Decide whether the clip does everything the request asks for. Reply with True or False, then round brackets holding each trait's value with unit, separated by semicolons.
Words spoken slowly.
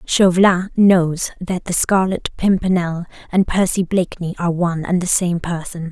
False (150 wpm)